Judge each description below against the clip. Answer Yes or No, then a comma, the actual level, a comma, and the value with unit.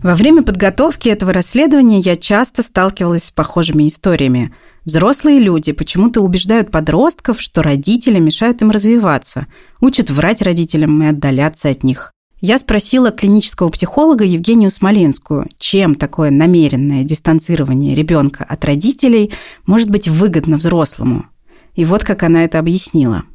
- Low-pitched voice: No, medium, 175 Hz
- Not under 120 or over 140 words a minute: Yes, average, 130 wpm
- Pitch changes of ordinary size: No, wide, 5.9 semitones